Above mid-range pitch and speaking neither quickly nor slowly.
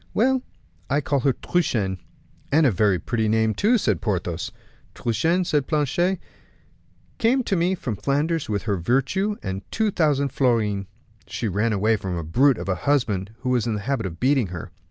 No: low, 125 Hz; average, 180 wpm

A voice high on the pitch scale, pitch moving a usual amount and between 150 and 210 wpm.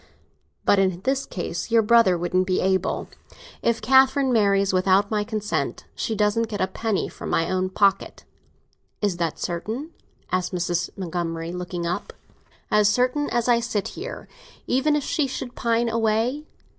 Yes: high, 210 Hz; average, 4.4 semitones; average, 160 wpm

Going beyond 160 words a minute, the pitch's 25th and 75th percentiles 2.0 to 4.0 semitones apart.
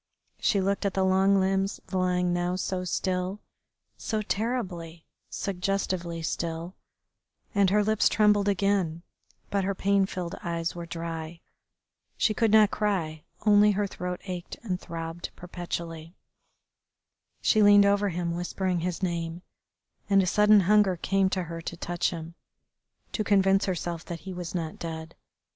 No: average, 145 wpm; average, 2.8 semitones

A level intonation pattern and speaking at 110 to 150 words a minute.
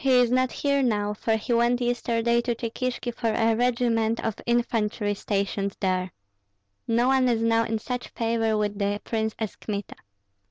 No: narrow, 2.2 semitones; average, 170 wpm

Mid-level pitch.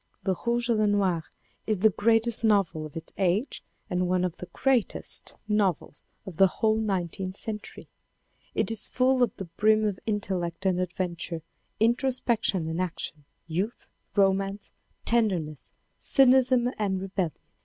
No: high, 195 Hz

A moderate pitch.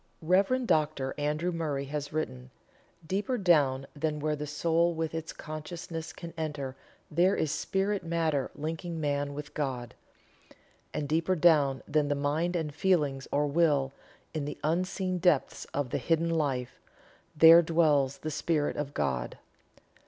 Yes: medium, 155 Hz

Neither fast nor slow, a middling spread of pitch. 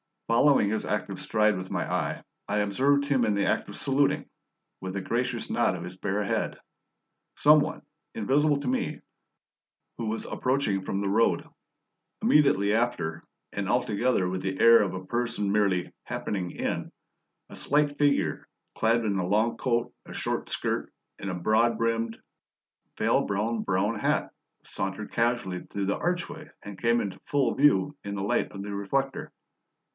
Yes: average, 165 wpm; average, 4.2 semitones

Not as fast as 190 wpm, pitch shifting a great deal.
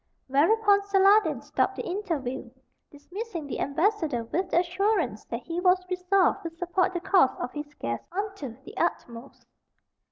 Yes: average, 150 wpm; wide, 5.8 semitones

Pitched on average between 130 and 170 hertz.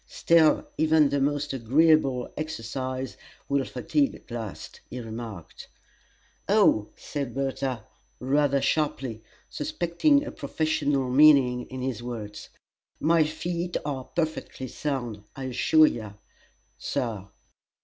Yes: low, 135 Hz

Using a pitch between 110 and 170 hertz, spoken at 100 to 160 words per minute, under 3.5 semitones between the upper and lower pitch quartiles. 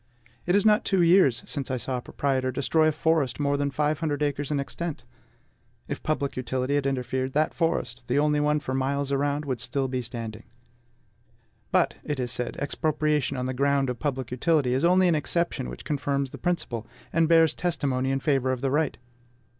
No: medium, 140 Hz; average, 195 wpm; average, 2.9 semitones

